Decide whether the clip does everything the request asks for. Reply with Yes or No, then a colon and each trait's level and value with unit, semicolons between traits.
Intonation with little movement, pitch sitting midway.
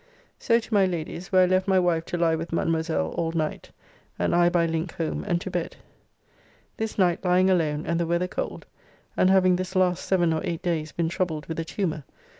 Yes: narrow, 2.2 semitones; medium, 175 Hz